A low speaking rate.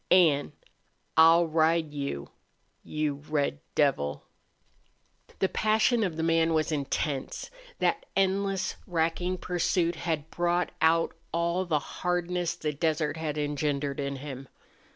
Yes: slow, 120 wpm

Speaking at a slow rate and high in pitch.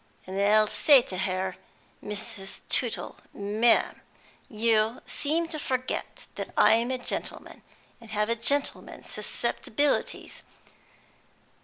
Yes: slow, 110 wpm; high, 225 Hz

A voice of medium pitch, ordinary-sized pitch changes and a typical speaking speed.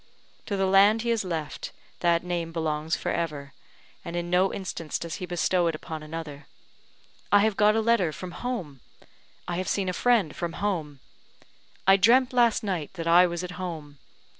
Yes: medium, 175 Hz; average, 3.5 semitones; average, 185 wpm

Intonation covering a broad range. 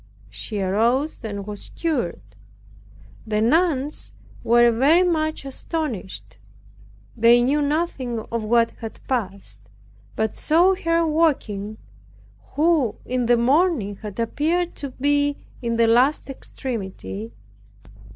Yes: wide, 5.9 semitones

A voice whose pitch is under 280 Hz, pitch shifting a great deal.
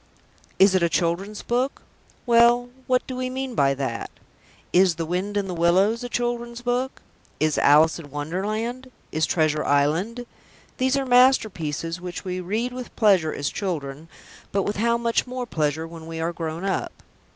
Yes: high, 190 Hz; wide, 6.8 semitones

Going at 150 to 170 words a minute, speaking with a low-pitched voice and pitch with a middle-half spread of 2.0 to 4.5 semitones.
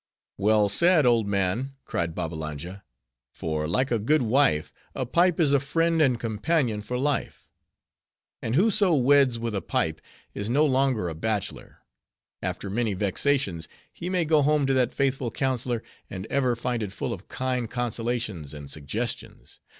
No: average, 160 wpm; low, 120 Hz; wide, 5.4 semitones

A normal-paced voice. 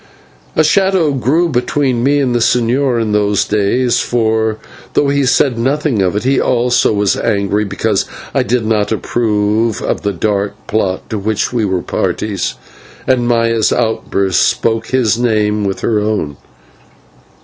Yes: average, 155 wpm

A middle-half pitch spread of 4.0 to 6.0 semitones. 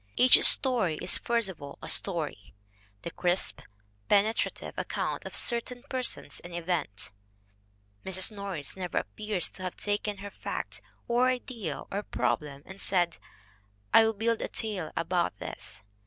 Yes: average, 4.6 semitones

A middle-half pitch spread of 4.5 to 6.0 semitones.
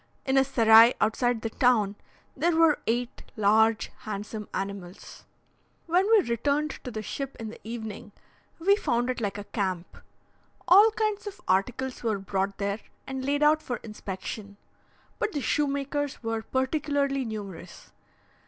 Yes: average, 5.1 semitones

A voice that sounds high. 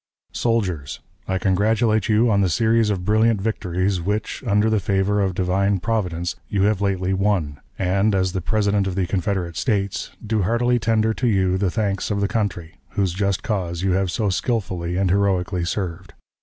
No: low, 100 Hz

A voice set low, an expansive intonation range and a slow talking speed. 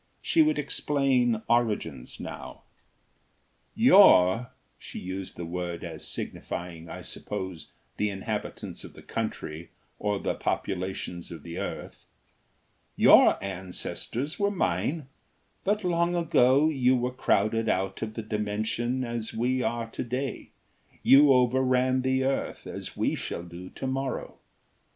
Yes: low, 115 Hz; wide, 5.8 semitones; slow, 130 wpm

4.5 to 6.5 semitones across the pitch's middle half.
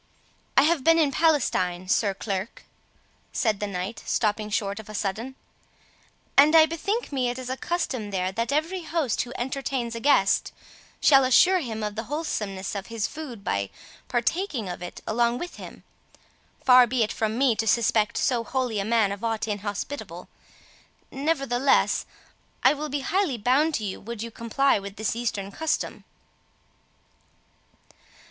Yes: average, 5.0 semitones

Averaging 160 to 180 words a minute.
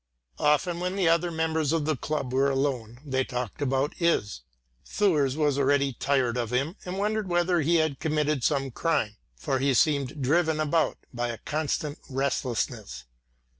Yes: average, 165 wpm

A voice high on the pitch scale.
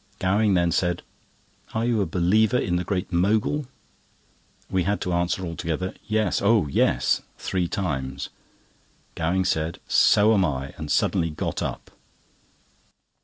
No: very low, 90 Hz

